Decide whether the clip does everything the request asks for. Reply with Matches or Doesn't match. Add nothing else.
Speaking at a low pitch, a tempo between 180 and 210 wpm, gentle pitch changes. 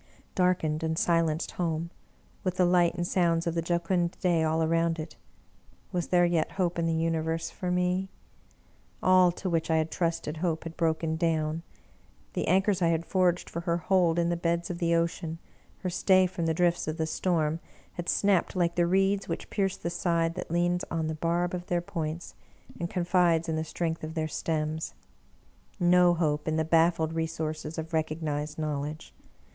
Doesn't match